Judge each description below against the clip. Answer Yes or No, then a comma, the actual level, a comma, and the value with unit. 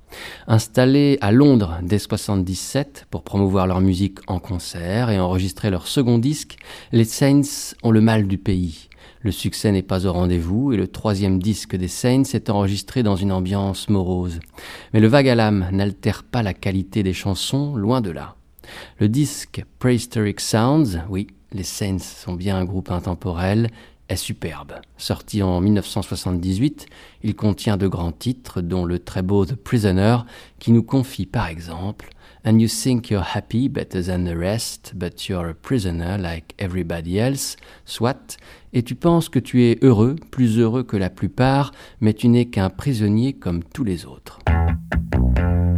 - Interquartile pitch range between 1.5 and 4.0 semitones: No, average, 4.4 semitones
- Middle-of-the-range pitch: No, low, 100 Hz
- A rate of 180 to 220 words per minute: No, average, 165 wpm